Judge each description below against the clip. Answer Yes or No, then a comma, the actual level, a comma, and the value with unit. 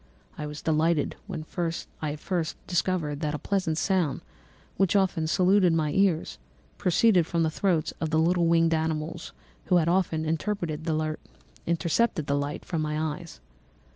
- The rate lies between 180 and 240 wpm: No, average, 145 wpm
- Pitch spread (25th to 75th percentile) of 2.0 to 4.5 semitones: Yes, narrow, 2.6 semitones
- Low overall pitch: No, medium, 165 Hz